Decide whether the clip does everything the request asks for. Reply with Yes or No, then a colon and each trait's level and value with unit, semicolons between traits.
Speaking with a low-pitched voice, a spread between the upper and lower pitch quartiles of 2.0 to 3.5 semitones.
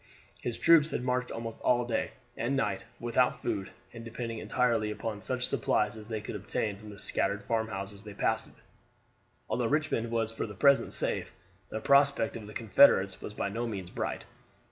Yes: low, 115 Hz; average, 2.9 semitones